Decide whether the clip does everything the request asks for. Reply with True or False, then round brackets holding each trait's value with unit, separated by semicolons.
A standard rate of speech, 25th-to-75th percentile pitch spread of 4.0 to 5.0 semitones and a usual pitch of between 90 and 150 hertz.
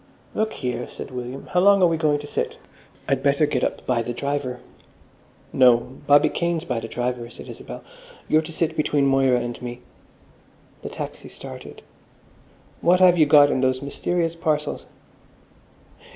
True (160 wpm; 4.3 semitones; 140 Hz)